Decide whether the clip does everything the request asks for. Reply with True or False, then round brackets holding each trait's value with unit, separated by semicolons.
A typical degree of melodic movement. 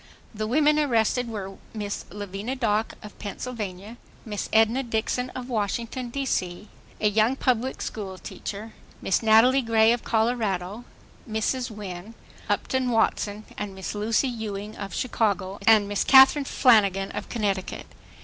True (3.1 semitones)